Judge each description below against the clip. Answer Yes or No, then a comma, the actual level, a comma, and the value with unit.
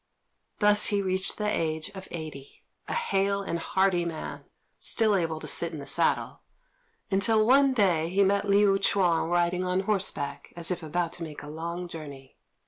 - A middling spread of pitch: Yes, average, 3.4 semitones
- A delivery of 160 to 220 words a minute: Yes, average, 175 wpm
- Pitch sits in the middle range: Yes, medium, 180 Hz